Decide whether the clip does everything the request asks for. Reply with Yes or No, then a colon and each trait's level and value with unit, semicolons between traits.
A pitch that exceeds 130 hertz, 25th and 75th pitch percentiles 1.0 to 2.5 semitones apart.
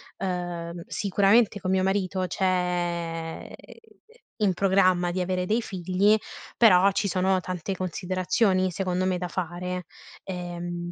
Yes: medium, 185 Hz; narrow, 1.4 semitones